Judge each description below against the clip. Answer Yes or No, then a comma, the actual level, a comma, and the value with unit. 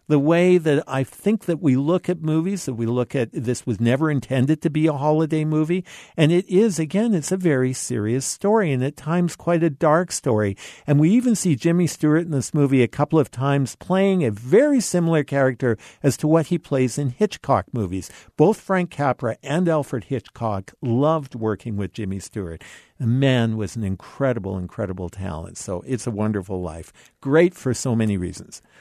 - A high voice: No, medium, 140 Hz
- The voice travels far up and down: Yes, wide, 6.1 semitones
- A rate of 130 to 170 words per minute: No, average, 195 wpm